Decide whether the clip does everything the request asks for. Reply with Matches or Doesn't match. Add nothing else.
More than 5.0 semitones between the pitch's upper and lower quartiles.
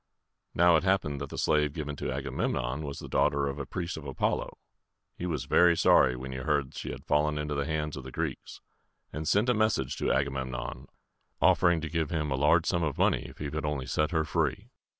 Doesn't match